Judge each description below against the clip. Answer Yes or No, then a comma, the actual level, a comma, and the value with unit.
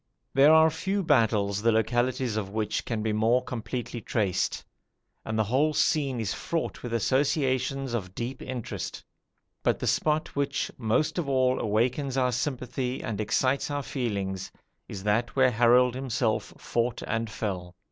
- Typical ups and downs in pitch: Yes, average, 3.5 semitones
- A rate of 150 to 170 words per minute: Yes, average, 155 wpm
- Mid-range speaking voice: No, low, 125 Hz